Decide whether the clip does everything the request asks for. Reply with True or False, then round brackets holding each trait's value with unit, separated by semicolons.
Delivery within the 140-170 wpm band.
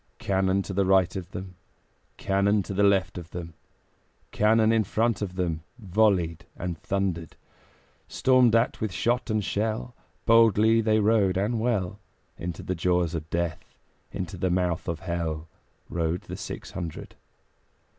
True (145 wpm)